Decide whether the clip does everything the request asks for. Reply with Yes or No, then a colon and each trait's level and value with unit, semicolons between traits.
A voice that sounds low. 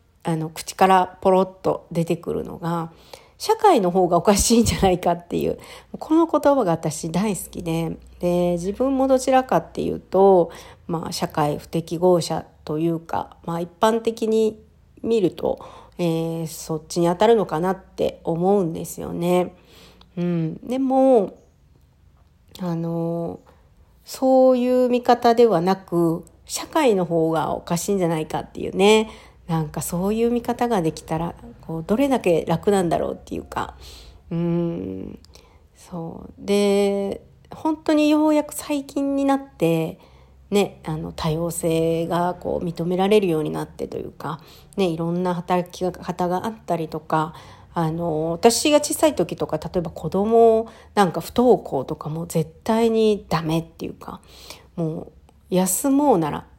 No: medium, 175 Hz